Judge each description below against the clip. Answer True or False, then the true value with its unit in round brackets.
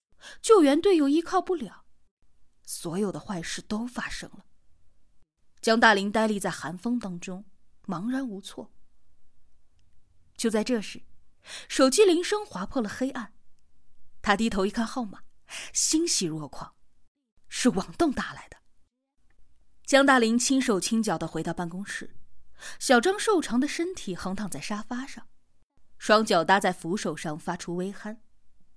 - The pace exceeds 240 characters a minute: False (205 characters per minute)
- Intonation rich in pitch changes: True (6.8 semitones)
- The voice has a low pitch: False (215 Hz)